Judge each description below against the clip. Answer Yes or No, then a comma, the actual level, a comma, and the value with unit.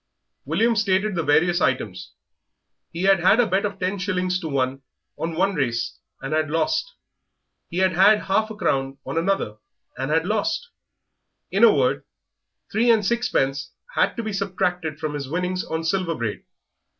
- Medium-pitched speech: Yes, medium, 180 Hz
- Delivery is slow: No, average, 170 wpm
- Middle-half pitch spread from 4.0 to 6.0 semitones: Yes, average, 4.8 semitones